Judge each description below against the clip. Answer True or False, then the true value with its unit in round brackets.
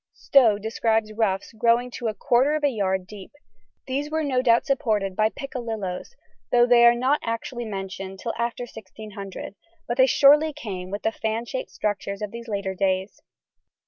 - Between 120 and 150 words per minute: False (175 wpm)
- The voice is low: False (225 Hz)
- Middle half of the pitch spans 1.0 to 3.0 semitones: False (3.8 semitones)